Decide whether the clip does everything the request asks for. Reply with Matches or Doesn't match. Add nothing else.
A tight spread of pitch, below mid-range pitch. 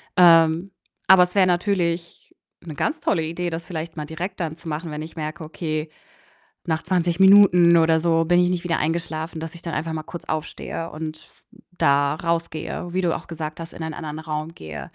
Doesn't match